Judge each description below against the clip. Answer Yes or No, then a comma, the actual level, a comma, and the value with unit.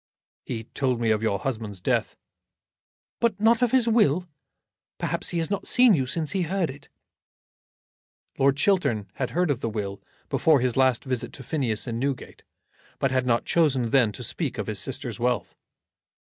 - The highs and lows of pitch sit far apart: Yes, wide, 6.5 semitones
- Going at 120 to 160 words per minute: No, average, 175 wpm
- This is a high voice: No, low, 135 Hz